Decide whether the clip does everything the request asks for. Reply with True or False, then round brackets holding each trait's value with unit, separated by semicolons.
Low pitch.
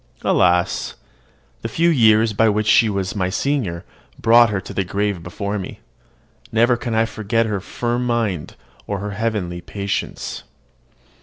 True (105 Hz)